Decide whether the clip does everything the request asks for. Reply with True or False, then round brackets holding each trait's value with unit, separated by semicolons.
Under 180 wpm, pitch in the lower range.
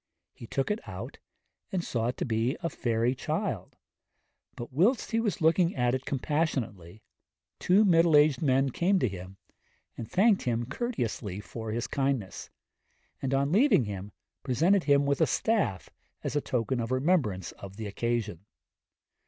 True (160 wpm; 130 Hz)